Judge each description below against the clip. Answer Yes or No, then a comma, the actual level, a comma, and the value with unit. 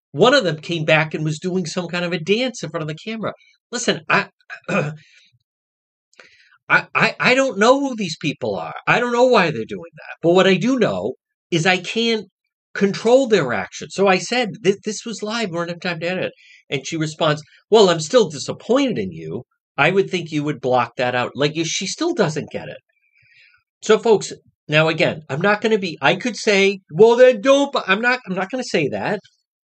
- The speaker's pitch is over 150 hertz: Yes, medium, 185 Hz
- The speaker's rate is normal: No, fast, 215 wpm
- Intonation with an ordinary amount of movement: No, wide, 5.8 semitones